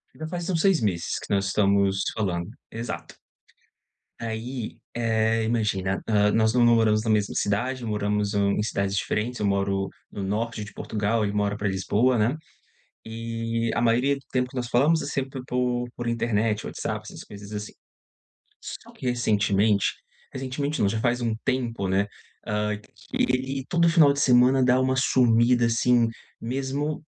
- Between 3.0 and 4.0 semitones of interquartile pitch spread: Yes, average, 3.4 semitones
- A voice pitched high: No, low, 115 Hz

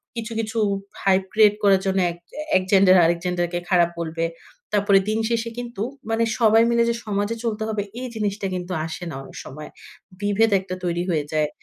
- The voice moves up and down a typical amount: Yes, average, 3.9 semitones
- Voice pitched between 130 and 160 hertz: No, high, 200 Hz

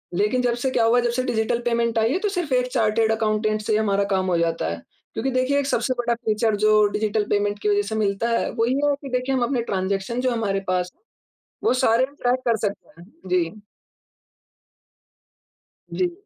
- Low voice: No, high, 225 Hz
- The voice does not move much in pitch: No, average, 3.3 semitones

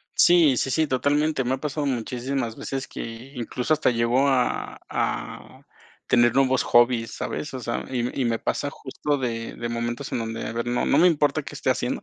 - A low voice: Yes, low, 130 Hz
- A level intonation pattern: No, average, 3.0 semitones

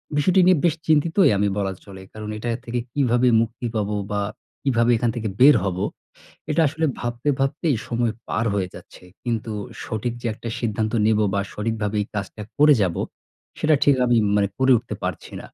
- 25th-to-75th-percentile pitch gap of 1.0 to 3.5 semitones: No, average, 4.3 semitones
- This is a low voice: Yes, low, 120 Hz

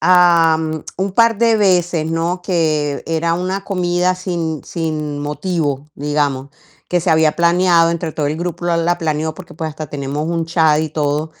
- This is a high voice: No, medium, 165 Hz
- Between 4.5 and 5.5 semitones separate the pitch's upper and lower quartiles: No, narrow, 2.4 semitones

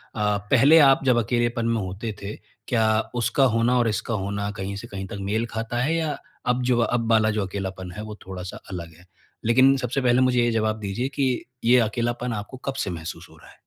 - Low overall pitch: Yes, low, 115 Hz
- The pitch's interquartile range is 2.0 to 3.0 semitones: No, average, 3.5 semitones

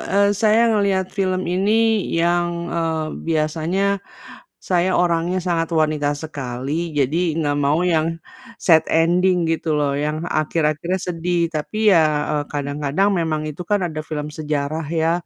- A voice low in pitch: No, medium, 165 Hz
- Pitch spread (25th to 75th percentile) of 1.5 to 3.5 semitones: Yes, average, 2.9 semitones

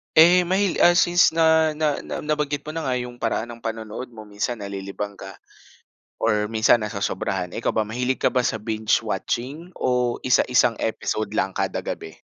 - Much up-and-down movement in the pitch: Yes, wide, 5.8 semitones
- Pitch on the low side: Yes, low, 120 Hz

